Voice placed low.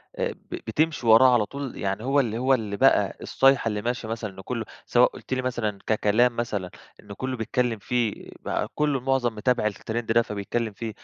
Yes: low, 115 Hz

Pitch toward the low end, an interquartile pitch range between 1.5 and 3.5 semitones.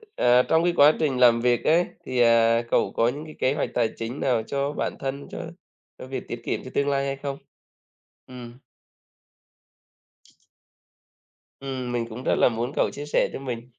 Yes: low, 130 Hz; average, 2.8 semitones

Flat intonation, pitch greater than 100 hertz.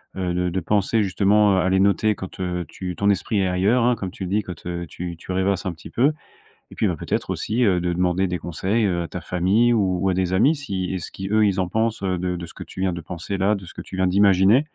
No: narrow, 2.3 semitones; very low, 95 Hz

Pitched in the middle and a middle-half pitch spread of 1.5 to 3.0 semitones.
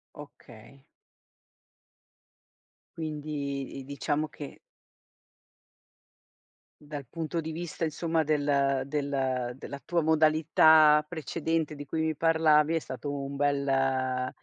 Yes: medium, 150 Hz; narrow, 2.4 semitones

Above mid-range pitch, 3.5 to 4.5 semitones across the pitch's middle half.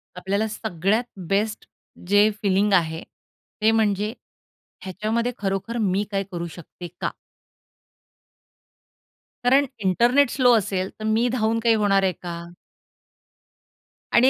No: high, 205 Hz; average, 3.1 semitones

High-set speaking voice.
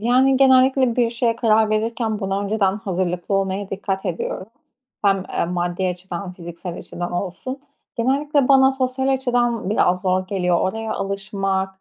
Yes: high, 200 Hz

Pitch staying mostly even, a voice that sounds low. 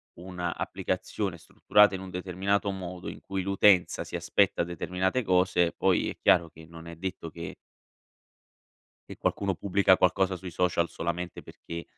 Yes: narrow, 2.0 semitones; very low, 90 Hz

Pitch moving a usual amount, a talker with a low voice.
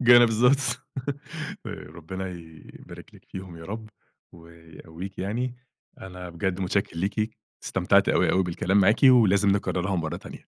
Yes: average, 3.9 semitones; very low, 95 Hz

